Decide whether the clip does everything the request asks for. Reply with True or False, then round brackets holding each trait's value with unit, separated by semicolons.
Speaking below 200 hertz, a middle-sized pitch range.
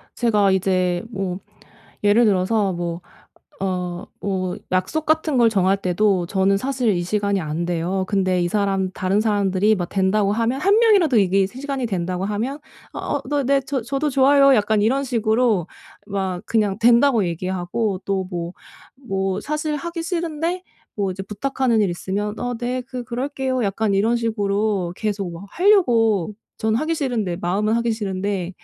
False (210 Hz; 4.8 semitones)